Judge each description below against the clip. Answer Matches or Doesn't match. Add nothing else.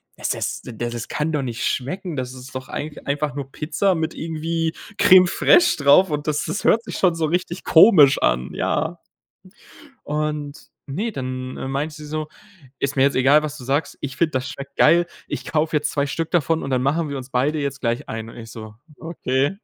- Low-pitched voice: Doesn't match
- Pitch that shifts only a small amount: Doesn't match